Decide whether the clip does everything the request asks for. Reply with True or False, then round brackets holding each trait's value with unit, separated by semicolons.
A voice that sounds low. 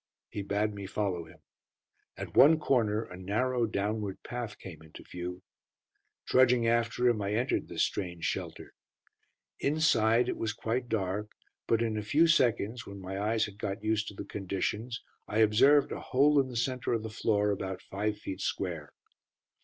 True (110 Hz)